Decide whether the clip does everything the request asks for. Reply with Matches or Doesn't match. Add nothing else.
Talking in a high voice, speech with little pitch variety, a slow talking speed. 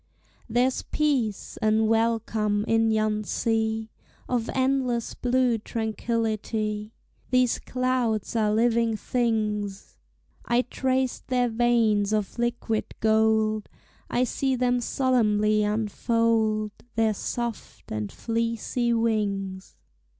Matches